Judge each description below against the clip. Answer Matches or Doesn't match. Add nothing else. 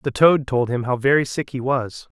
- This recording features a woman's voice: Doesn't match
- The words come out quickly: Matches